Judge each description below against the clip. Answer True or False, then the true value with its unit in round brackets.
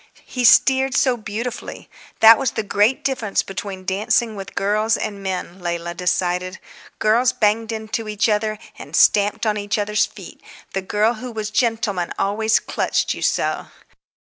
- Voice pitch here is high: True (215 Hz)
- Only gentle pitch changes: True (2.3 semitones)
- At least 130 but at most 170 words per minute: True (155 wpm)